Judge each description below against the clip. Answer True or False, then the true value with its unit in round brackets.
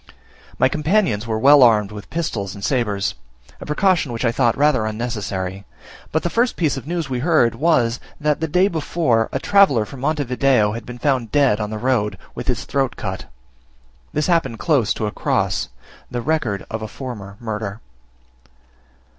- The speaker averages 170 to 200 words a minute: True (180 wpm)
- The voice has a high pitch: False (125 Hz)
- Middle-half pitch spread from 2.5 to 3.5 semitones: False (5.6 semitones)